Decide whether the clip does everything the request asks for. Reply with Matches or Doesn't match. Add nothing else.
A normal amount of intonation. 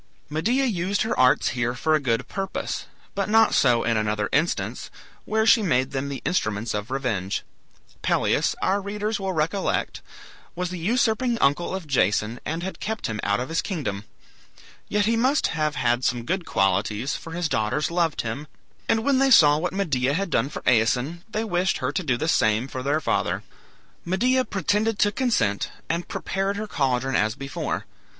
Doesn't match